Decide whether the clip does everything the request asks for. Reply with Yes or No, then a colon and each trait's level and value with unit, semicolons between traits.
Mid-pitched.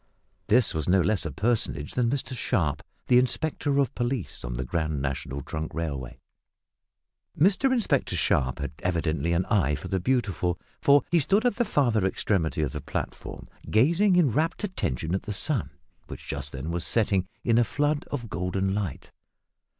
No: low, 100 Hz